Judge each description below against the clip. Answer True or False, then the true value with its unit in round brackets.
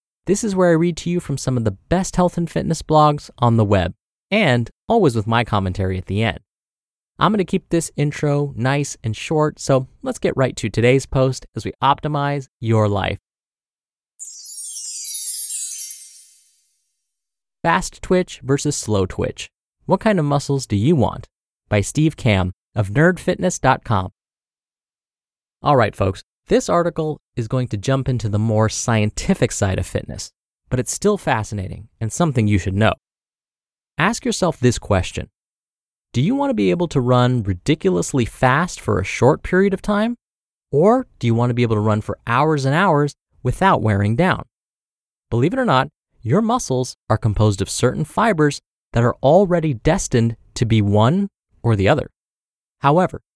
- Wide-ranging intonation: True (7.5 semitones)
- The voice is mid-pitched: False (130 Hz)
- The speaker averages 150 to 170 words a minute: True (165 wpm)